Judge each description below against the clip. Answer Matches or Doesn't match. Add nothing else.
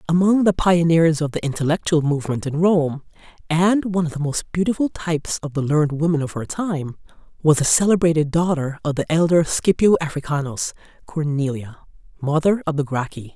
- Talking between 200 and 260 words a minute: Doesn't match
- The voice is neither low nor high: Matches